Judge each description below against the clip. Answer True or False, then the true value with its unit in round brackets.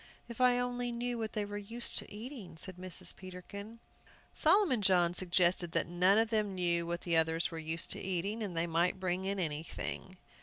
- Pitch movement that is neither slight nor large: True (4.3 semitones)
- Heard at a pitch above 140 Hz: True (185 Hz)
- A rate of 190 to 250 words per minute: True (195 wpm)